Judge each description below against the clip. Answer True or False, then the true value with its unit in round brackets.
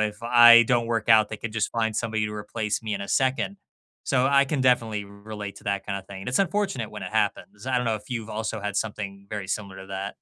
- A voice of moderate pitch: False (110 Hz)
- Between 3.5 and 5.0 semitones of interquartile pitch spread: False (2.6 semitones)